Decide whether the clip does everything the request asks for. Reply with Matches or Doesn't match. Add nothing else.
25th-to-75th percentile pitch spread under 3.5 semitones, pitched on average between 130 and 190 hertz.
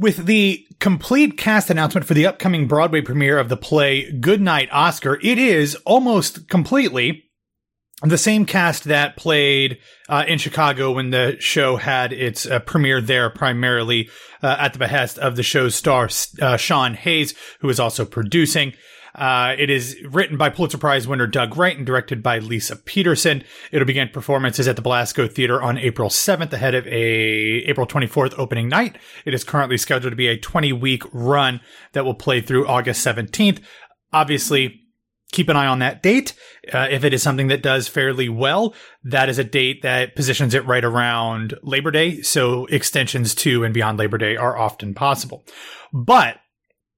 Doesn't match